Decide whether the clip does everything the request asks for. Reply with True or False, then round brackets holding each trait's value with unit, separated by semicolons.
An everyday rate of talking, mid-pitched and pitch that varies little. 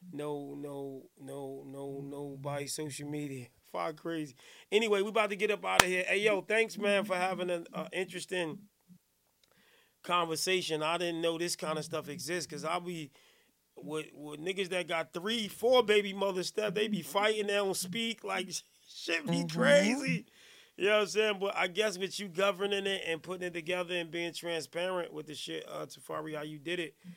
False (190 wpm; 175 Hz; 4.6 semitones)